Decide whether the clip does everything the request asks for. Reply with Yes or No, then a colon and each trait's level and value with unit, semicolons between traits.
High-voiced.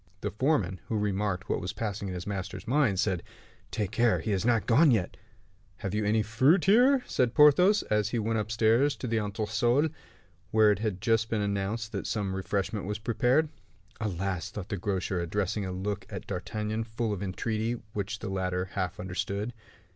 No: low, 105 Hz